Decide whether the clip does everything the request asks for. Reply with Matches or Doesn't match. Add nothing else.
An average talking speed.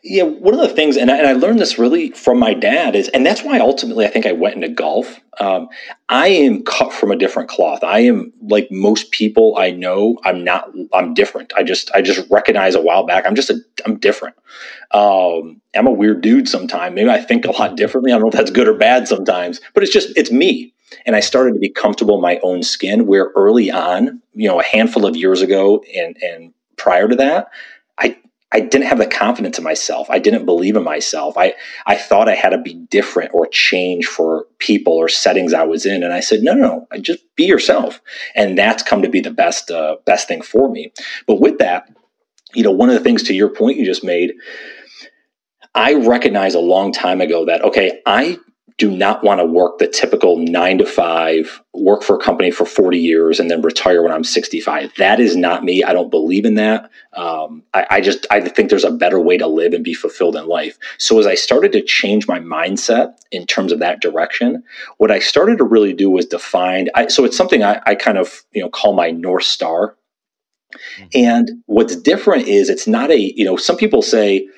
Doesn't match